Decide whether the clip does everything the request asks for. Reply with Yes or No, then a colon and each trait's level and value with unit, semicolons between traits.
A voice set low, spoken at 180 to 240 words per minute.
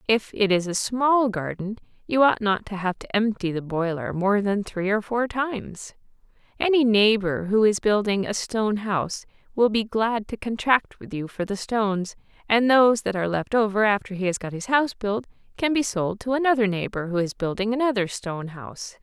No: high, 210 Hz; average, 200 wpm